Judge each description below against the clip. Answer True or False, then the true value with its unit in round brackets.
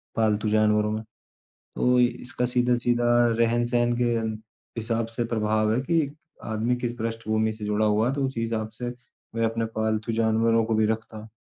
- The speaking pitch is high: False (115 Hz)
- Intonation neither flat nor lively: False (1.8 semitones)